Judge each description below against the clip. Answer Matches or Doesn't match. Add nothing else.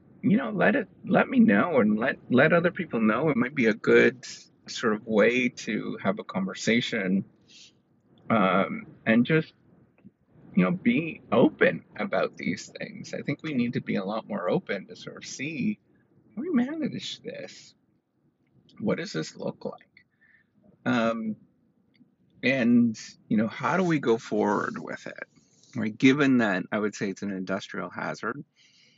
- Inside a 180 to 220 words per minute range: Doesn't match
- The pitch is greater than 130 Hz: Matches